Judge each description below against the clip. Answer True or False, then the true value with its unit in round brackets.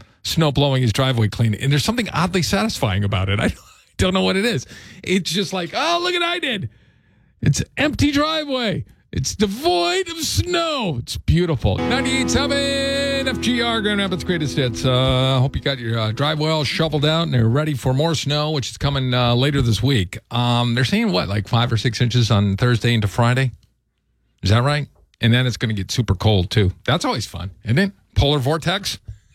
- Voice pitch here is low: True (130 Hz)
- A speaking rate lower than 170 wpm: False (200 wpm)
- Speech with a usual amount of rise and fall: False (8.3 semitones)